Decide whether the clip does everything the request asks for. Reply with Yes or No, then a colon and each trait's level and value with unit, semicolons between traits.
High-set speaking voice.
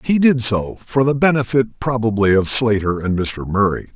No: low, 115 Hz